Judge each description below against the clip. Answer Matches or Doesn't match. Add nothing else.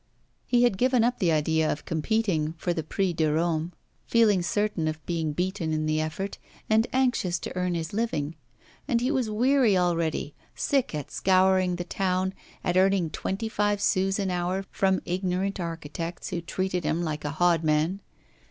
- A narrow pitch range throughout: Doesn't match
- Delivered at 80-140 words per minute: Doesn't match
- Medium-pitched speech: Matches